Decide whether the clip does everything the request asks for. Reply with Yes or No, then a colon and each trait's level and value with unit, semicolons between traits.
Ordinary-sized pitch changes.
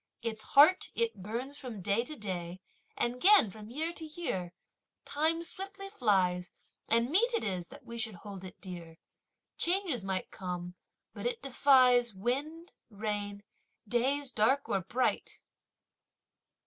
No: wide, 7.5 semitones